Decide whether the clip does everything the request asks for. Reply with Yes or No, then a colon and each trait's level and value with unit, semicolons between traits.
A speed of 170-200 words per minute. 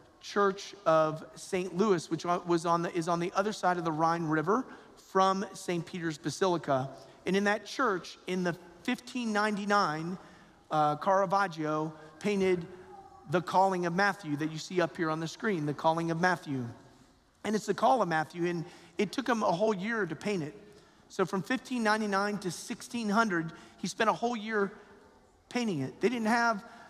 Yes: average, 175 wpm